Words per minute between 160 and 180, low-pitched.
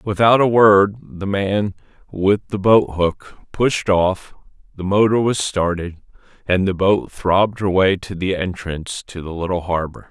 Yes: average, 165 wpm; very low, 95 Hz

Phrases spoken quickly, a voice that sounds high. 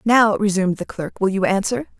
Yes: fast, 210 wpm; high, 200 Hz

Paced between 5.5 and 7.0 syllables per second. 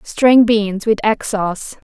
No: 3.5 syllables/s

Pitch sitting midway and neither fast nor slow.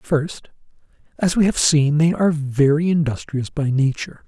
Yes: medium, 150 Hz; average, 155 wpm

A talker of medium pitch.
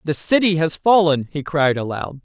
Yes: medium, 160 Hz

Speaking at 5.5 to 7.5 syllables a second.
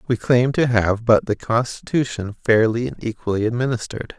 No: 5.2 syllables/s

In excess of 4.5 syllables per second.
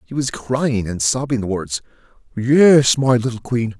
No: 4.2 syllables/s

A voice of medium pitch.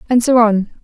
No: high, 230 Hz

